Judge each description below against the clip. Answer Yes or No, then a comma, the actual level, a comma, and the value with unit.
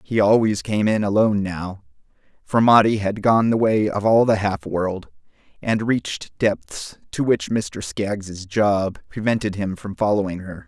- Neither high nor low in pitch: No, low, 105 Hz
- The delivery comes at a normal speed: Yes, average, 170 wpm